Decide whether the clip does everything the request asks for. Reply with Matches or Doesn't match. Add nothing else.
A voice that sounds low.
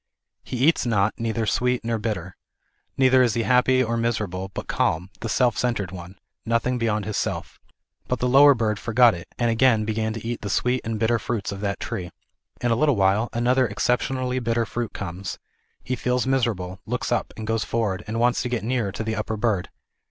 Matches